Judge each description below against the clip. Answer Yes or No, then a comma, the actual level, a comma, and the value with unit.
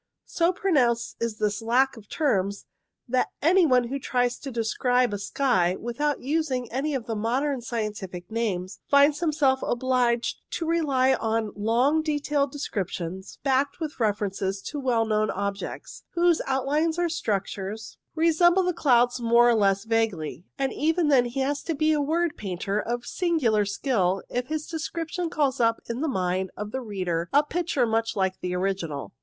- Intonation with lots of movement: Yes, wide, 5.8 semitones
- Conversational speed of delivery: Yes, average, 170 wpm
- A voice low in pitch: No, high, 245 Hz